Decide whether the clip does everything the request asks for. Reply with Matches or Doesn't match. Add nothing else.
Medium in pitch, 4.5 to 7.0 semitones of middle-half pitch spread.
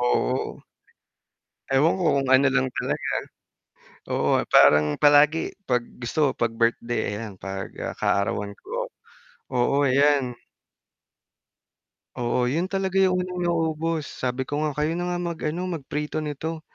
Matches